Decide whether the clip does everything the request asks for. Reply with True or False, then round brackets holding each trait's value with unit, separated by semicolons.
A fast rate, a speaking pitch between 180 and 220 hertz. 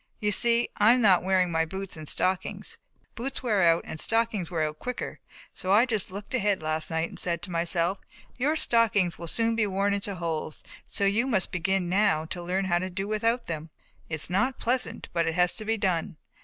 True (210 wpm; 190 Hz)